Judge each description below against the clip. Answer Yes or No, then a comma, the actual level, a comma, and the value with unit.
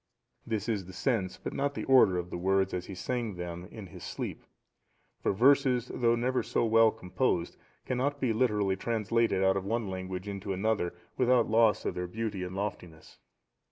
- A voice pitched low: Yes, low, 105 Hz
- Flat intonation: No, average, 4.0 semitones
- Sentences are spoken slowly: No, average, 185 wpm